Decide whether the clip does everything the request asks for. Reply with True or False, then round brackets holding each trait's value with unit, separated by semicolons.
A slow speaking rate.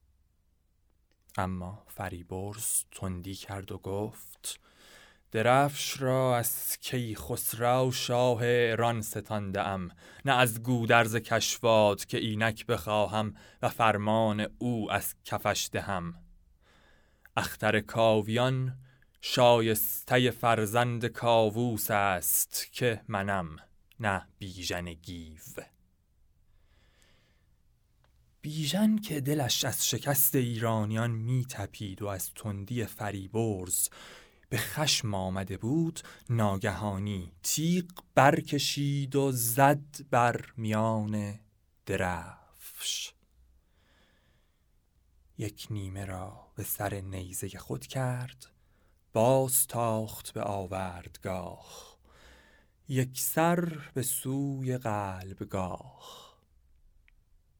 True (85 wpm)